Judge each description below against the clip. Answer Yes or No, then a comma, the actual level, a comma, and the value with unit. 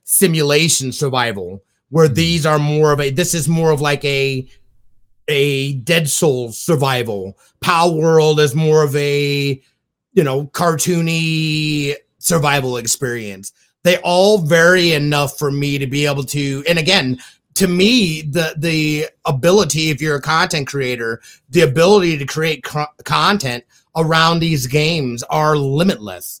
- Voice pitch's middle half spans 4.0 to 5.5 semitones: No, average, 3.1 semitones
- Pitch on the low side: No, medium, 150 Hz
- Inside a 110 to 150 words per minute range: Yes, average, 140 wpm